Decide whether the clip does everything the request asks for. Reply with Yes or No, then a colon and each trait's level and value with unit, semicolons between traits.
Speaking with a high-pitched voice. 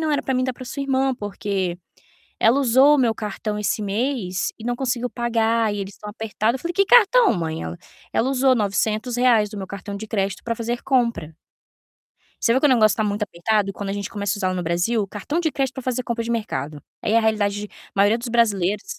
Yes: high, 225 Hz